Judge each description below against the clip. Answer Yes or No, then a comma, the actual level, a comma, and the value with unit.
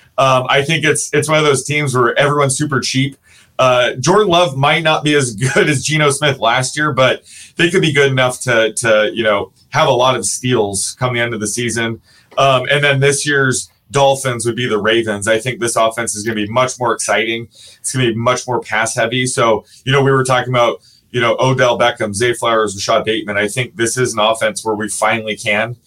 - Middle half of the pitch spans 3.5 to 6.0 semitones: Yes, average, 3.8 semitones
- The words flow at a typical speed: No, fast, 235 wpm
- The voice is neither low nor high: No, low, 125 Hz